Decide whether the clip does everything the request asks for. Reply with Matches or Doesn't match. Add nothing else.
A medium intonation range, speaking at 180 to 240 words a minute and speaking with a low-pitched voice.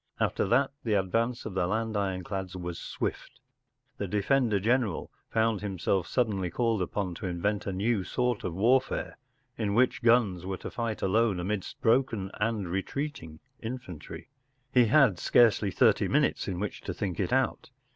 Doesn't match